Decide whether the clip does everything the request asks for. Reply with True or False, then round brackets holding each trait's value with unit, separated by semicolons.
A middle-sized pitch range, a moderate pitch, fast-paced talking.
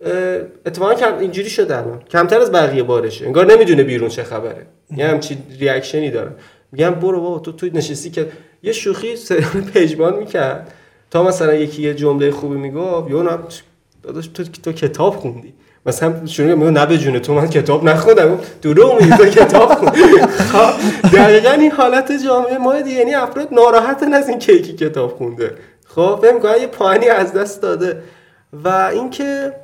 False (9.0 semitones; 180 Hz; 160 wpm)